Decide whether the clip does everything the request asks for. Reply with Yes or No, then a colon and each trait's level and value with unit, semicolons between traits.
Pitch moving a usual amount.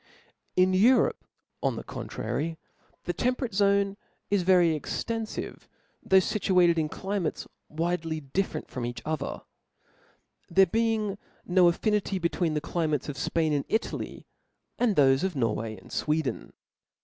Yes: average, 4.4 semitones